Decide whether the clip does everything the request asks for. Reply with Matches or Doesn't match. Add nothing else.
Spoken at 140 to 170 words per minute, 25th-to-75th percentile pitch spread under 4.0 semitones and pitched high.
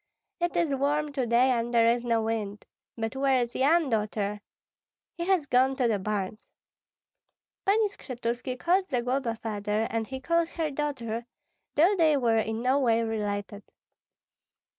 Doesn't match